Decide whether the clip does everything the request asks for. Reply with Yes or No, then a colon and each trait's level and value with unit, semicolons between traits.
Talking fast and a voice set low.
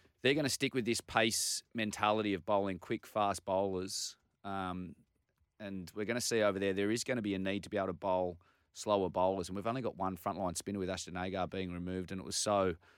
Yes: fast, 235 wpm; very low, 95 Hz